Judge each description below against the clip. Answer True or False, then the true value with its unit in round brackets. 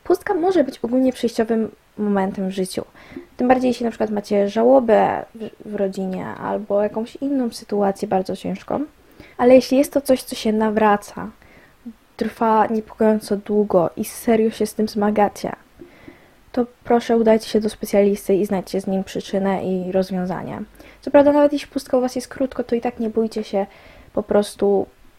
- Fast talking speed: True (165 wpm)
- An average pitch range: True (3.5 semitones)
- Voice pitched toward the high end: True (220 Hz)